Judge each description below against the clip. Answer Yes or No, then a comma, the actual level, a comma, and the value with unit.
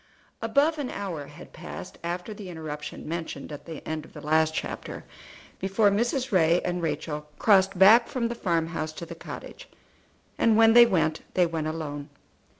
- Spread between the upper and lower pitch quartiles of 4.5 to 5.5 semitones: Yes, average, 5.2 semitones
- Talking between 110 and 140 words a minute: No, average, 175 wpm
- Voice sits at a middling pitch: Yes, medium, 175 Hz